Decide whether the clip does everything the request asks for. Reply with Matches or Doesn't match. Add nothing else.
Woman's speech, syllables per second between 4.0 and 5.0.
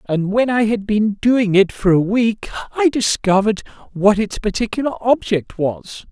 Doesn't match